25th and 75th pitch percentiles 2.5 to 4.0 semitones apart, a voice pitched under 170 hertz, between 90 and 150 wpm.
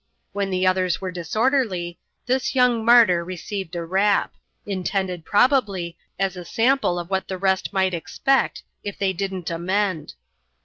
No: average, 2.8 semitones; high, 190 Hz; average, 145 wpm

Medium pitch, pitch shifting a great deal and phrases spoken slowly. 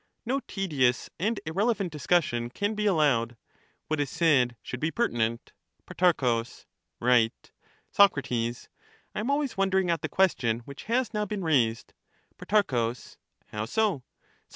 Yes: medium, 160 Hz; wide, 8.9 semitones; slow, 130 wpm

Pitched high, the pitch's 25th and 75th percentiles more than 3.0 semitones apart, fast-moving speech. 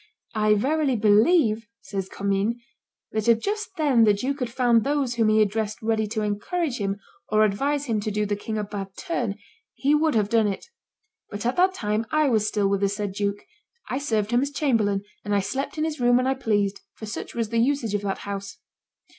Yes: high, 220 Hz; average, 4.4 semitones; fast, 215 wpm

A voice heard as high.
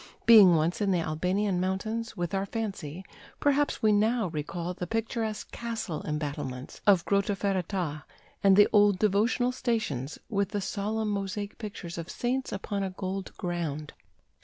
Yes: high, 195 Hz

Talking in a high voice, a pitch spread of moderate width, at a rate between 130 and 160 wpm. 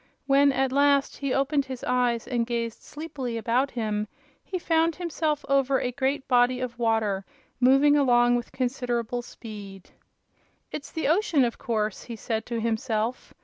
Yes: very high, 250 Hz; average, 3.1 semitones; average, 155 wpm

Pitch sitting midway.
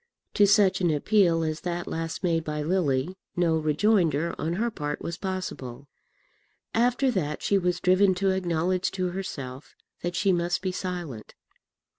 Yes: medium, 175 Hz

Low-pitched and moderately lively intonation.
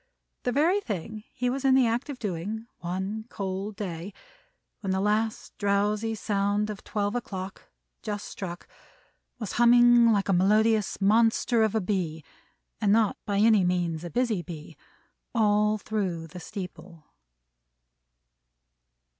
No: high, 210 Hz; average, 3.0 semitones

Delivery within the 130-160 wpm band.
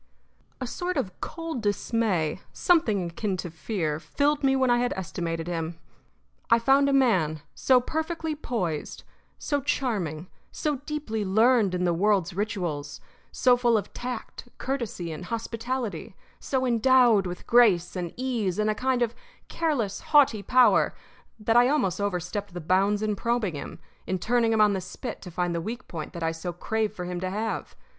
No: average, 170 wpm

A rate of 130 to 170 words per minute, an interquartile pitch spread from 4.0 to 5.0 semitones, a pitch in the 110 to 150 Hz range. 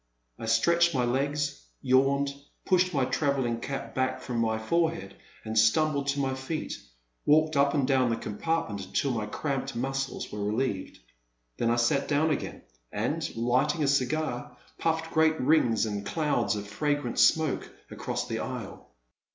Yes: average, 155 wpm; average, 4.5 semitones; low, 135 Hz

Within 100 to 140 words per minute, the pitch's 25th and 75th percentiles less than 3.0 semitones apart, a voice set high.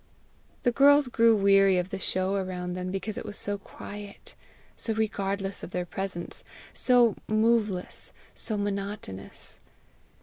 Yes: slow, 135 wpm; narrow, 2.5 semitones; high, 200 Hz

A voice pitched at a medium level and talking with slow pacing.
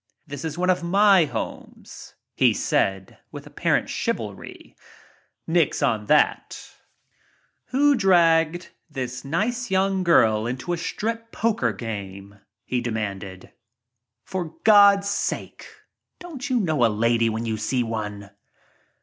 Yes: medium, 155 Hz; slow, 130 wpm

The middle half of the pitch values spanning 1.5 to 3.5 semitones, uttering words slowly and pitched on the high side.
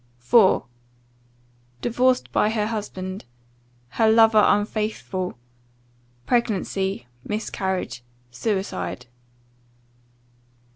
Yes: average, 2.9 semitones; slow, 60 wpm; high, 210 Hz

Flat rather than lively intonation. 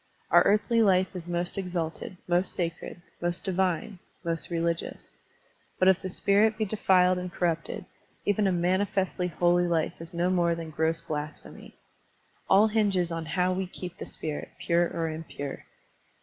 Yes: narrow, 2.2 semitones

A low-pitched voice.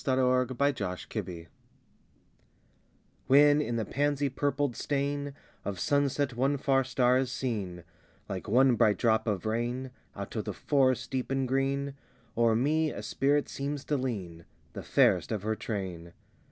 Yes: low, 130 Hz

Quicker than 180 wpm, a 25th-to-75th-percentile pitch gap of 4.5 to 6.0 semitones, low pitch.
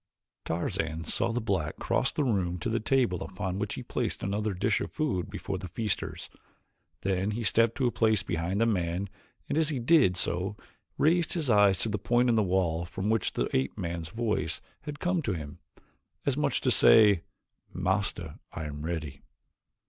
Yes: average, 190 wpm; average, 4.8 semitones; low, 100 Hz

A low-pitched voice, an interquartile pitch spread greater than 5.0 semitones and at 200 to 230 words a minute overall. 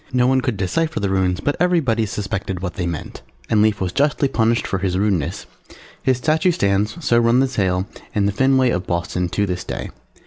Yes: low, 105 Hz; wide, 5.6 semitones; fast, 205 wpm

